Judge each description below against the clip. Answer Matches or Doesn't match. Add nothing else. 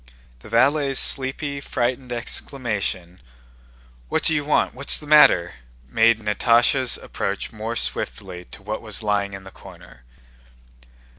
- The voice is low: Matches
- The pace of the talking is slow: Matches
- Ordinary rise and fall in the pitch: Matches